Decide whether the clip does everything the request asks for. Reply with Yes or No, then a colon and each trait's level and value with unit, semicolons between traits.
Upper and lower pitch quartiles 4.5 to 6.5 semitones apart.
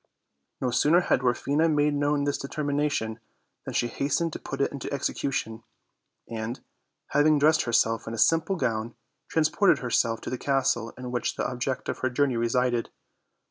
No: average, 3.7 semitones